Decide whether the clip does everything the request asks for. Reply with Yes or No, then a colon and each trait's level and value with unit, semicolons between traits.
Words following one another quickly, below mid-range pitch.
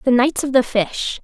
No: fast, 245 wpm; very high, 255 Hz